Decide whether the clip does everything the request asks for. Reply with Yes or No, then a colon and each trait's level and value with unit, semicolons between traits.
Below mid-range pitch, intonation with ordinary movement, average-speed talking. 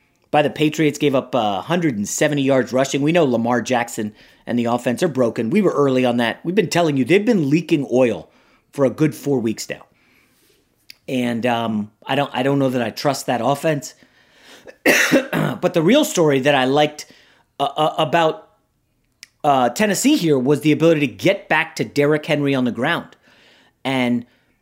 No: medium, 145 Hz; average, 3.9 semitones; average, 175 wpm